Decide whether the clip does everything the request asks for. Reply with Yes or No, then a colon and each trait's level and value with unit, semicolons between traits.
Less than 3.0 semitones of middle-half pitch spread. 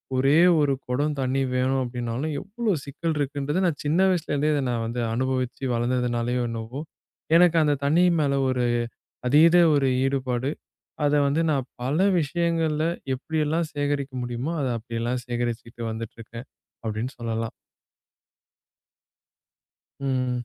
No: average, 3.5 semitones